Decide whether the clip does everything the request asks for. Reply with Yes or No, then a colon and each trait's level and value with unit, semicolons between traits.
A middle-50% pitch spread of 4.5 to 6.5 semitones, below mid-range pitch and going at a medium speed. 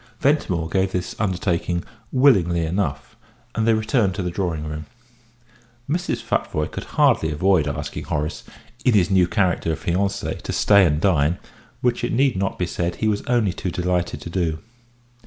No: average, 3.6 semitones; very low, 90 Hz; average, 170 wpm